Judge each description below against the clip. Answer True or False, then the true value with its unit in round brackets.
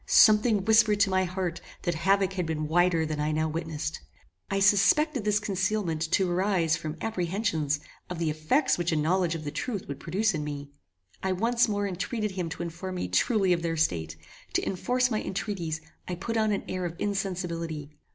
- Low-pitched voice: False (180 Hz)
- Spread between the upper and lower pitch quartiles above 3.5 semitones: True (4.1 semitones)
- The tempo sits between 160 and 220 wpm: True (190 wpm)